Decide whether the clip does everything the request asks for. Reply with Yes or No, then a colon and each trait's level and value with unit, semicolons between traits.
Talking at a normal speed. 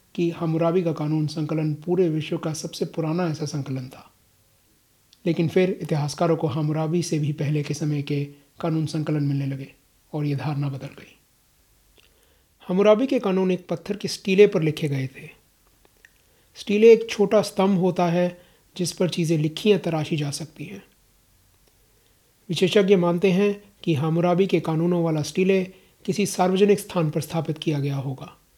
Yes: average, 160 wpm